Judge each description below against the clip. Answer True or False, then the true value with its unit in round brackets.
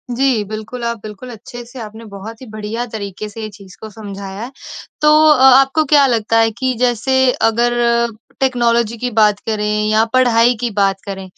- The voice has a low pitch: False (225 Hz)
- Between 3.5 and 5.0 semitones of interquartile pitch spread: False (2.8 semitones)